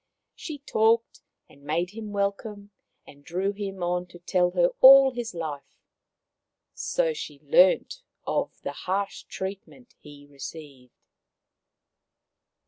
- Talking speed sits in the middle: No, slow, 120 wpm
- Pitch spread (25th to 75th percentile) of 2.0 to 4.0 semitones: No, average, 5.3 semitones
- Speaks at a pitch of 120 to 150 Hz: No, high, 190 Hz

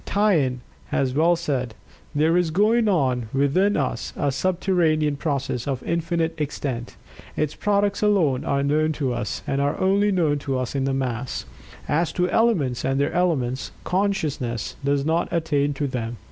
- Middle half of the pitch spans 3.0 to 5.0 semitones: Yes, average, 4.6 semitones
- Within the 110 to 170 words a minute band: Yes, average, 160 wpm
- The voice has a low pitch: No, medium, 145 Hz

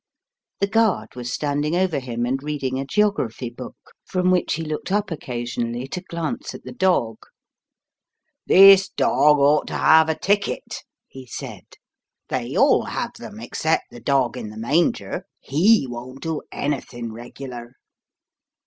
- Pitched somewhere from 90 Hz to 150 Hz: Yes, medium, 140 Hz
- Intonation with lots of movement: Yes, wide, 6.4 semitones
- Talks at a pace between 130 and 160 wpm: Yes, average, 150 wpm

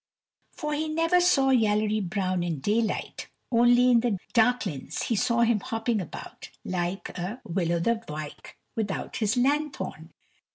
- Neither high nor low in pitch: No, high, 225 Hz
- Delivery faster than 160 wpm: No, average, 150 wpm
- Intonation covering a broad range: No, average, 4.9 semitones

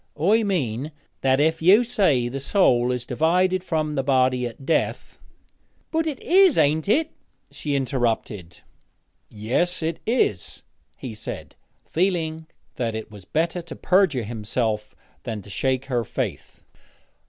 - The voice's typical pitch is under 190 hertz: Yes, medium, 140 Hz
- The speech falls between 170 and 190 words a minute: No, average, 140 wpm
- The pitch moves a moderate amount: No, wide, 6.8 semitones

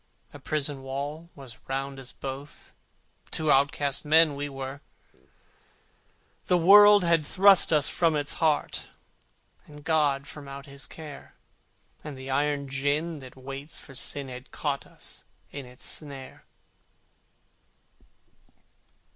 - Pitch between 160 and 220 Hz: No, medium, 145 Hz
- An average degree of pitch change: No, narrow, 2.2 semitones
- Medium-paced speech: No, slow, 125 wpm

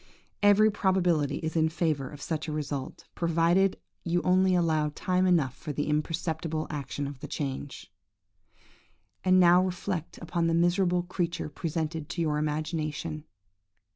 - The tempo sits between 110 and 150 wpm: Yes, average, 140 wpm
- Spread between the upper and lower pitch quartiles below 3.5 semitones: Yes, average, 2.8 semitones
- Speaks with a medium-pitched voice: Yes, medium, 165 Hz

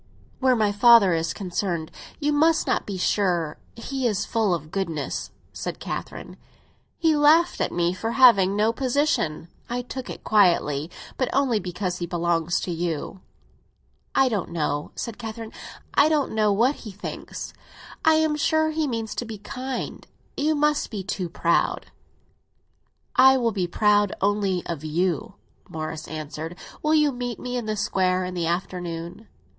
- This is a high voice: Yes, high, 205 Hz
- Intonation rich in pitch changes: Yes, wide, 6.6 semitones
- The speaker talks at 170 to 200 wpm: No, average, 160 wpm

